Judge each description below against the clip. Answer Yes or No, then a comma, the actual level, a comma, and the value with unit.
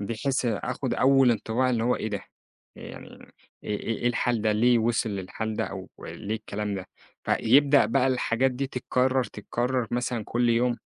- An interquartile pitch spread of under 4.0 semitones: Yes, average, 2.7 semitones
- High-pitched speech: No, low, 120 Hz